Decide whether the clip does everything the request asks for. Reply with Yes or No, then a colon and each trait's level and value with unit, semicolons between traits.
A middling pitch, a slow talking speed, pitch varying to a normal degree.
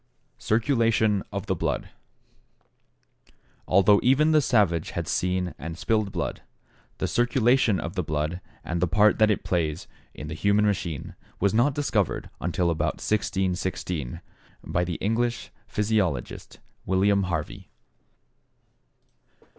No: low, 100 Hz; slow, 125 wpm; average, 4.1 semitones